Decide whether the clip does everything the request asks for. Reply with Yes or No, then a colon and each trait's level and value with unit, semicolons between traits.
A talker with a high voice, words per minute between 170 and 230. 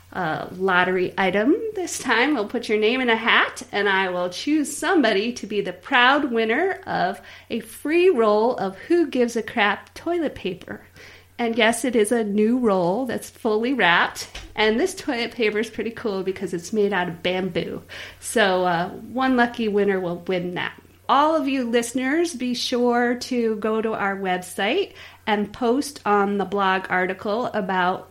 Yes: high, 225 Hz; average, 175 wpm